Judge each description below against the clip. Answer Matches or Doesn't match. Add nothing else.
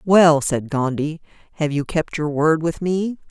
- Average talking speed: Matches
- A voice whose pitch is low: Doesn't match